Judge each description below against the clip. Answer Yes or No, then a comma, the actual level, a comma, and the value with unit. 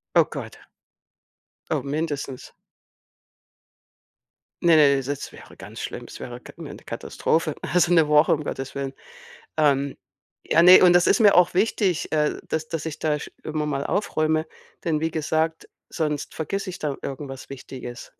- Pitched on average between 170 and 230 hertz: No, medium, 155 Hz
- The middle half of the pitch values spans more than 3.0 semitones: No, average, 2.7 semitones